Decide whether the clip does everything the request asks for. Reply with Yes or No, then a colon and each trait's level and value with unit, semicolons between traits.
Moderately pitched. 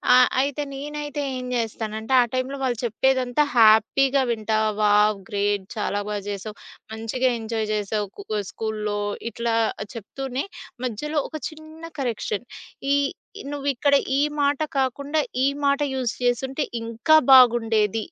No: high, 240 Hz